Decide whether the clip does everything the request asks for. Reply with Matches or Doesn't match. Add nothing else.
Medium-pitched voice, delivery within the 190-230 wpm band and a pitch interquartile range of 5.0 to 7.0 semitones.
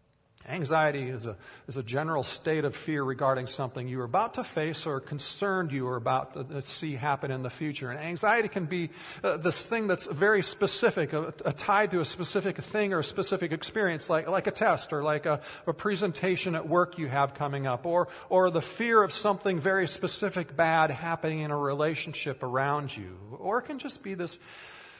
Matches